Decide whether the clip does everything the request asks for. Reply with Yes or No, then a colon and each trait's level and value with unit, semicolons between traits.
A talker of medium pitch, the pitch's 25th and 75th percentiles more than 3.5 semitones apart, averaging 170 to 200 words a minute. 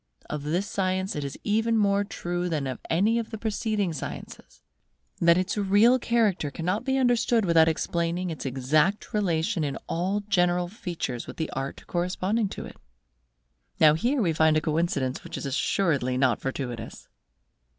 No: medium, 175 Hz; average, 5.1 semitones; average, 160 wpm